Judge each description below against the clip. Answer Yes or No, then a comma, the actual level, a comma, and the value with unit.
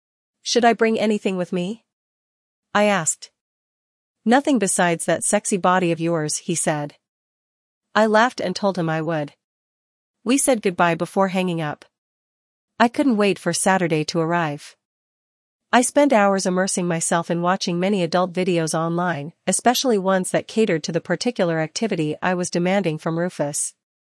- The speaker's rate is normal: Yes, average, 150 wpm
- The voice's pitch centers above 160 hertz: Yes, medium, 185 Hz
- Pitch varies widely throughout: No, average, 3.9 semitones